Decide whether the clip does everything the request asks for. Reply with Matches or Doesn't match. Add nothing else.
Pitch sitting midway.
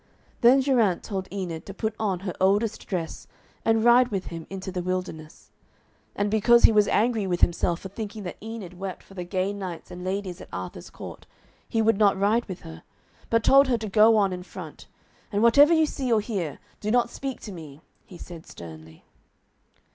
Doesn't match